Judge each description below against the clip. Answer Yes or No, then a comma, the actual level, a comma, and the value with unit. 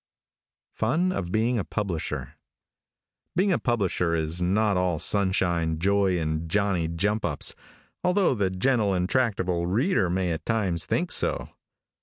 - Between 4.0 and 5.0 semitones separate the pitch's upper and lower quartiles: Yes, average, 4.3 semitones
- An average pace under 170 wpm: Yes, average, 140 wpm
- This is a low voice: Yes, very low, 95 Hz